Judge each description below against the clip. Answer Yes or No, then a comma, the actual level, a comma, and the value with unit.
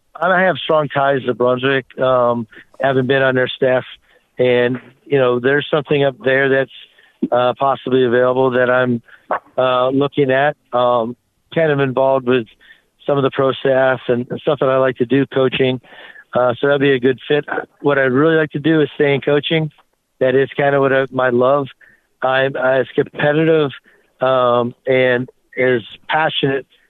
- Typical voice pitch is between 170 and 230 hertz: No, low, 130 Hz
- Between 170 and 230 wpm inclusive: Yes, average, 175 wpm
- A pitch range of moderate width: No, narrow, 1.9 semitones